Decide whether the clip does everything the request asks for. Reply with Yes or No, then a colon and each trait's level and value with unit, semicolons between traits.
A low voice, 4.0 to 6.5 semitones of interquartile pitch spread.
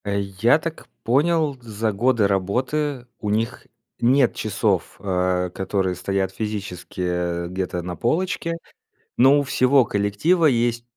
Yes: low, 110 Hz; wide, 5.6 semitones